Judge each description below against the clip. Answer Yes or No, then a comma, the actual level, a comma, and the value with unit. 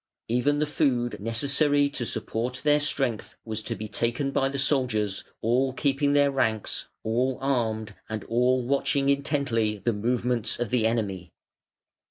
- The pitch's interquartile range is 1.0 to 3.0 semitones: No, average, 3.7 semitones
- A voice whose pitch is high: No, low, 125 Hz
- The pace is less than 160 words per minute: Yes, average, 150 wpm